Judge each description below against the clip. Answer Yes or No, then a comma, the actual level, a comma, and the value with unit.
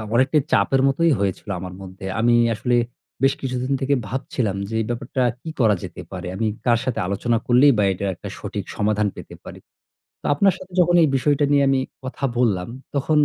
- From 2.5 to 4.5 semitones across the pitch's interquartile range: No, average, 4.9 semitones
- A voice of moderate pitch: No, low, 125 Hz